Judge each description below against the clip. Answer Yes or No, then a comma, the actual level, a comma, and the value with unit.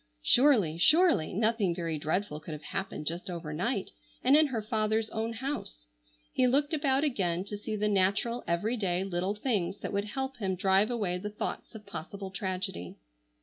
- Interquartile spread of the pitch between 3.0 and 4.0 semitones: No, average, 4.7 semitones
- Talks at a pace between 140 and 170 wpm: No, average, 180 wpm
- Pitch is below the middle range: No, high, 200 Hz